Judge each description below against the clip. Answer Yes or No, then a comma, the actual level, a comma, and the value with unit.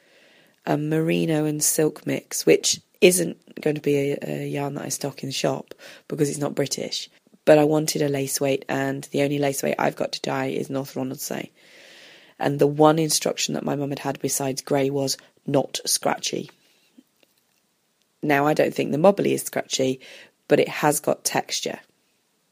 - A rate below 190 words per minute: Yes, average, 180 wpm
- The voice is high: No, medium, 140 Hz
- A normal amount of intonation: No, narrow, 2.1 semitones